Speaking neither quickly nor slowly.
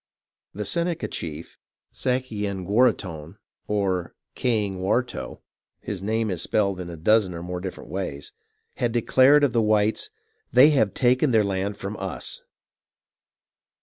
No: slow, 130 wpm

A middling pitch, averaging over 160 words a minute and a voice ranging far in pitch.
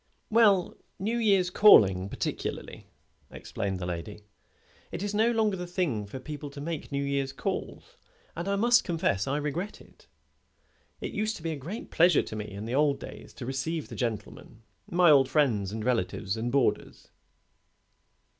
Yes: medium, 145 Hz; average, 170 wpm; wide, 8.2 semitones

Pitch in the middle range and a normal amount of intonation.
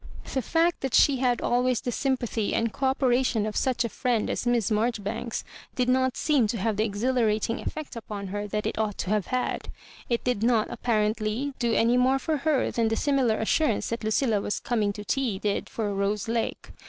No: high, 235 Hz; average, 3.2 semitones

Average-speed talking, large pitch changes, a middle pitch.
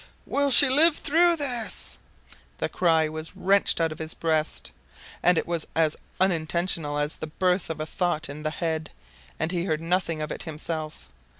No: average, 175 wpm; average, 3.1 semitones; medium, 165 Hz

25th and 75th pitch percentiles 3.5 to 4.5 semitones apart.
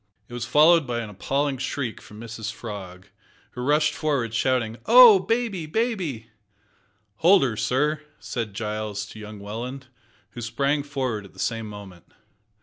No: wide, 5.5 semitones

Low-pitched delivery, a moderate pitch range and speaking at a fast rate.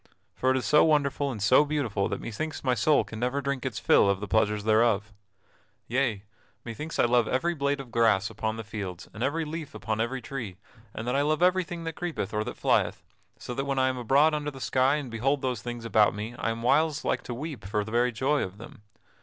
Yes: low, 125 Hz; average, 4.6 semitones; fast, 230 wpm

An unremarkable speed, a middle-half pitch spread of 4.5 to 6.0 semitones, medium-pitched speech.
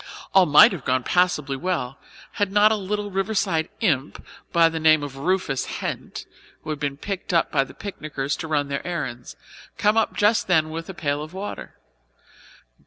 Yes: average, 175 wpm; average, 5.0 semitones; medium, 160 Hz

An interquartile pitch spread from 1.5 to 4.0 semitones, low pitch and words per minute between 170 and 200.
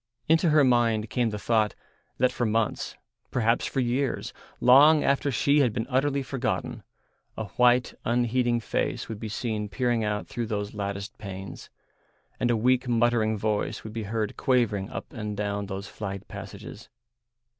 No: average, 3.0 semitones; low, 115 Hz; average, 160 wpm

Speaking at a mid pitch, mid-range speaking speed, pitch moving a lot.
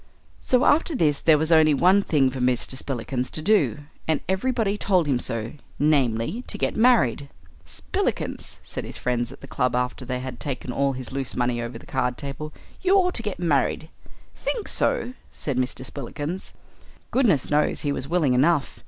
Yes: medium, 145 Hz; average, 180 wpm; wide, 6.2 semitones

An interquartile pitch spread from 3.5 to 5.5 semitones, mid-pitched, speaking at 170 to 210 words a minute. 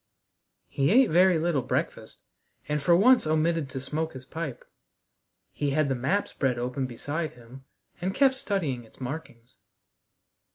No: average, 4.6 semitones; medium, 150 Hz; average, 150 wpm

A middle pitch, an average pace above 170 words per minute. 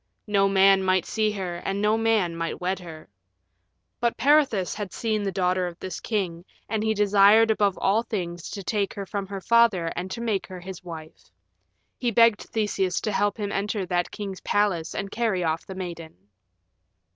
No: high, 195 Hz; average, 180 wpm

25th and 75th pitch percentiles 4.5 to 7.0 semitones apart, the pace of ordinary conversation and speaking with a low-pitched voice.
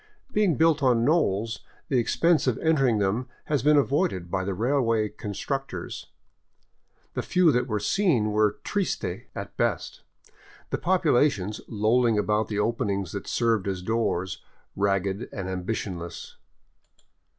No: wide, 5.6 semitones; slow, 130 wpm; low, 110 Hz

